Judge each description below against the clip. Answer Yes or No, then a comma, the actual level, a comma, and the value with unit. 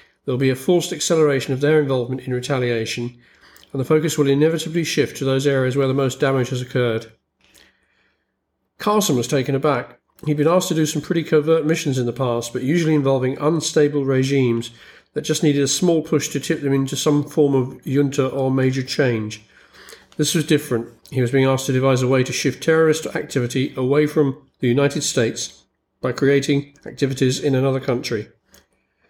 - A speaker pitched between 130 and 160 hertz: Yes, low, 135 Hz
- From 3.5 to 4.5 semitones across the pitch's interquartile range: No, average, 2.9 semitones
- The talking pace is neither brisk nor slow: Yes, average, 185 wpm